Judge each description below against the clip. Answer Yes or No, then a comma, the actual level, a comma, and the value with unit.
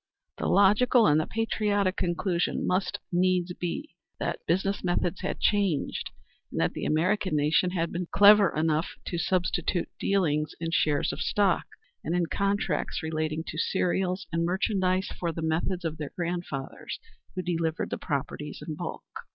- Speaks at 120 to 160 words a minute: Yes, average, 155 wpm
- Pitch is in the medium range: Yes, medium, 175 Hz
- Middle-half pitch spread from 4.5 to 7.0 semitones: No, average, 3.0 semitones